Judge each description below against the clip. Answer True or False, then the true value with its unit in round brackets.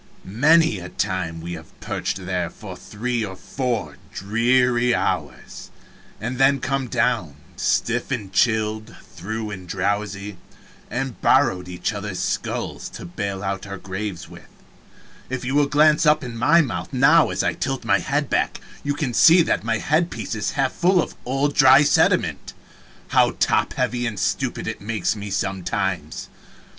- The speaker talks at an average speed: True (160 wpm)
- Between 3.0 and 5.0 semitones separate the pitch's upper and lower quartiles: False (5.6 semitones)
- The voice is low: True (110 Hz)